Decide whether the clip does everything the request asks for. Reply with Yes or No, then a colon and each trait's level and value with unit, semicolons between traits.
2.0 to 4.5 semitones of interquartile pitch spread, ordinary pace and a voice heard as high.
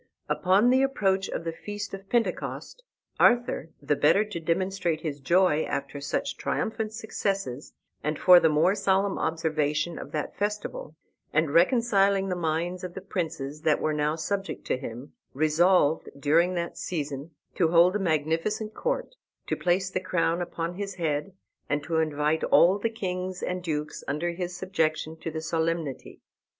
No: average, 3.8 semitones; average, 160 wpm; medium, 170 Hz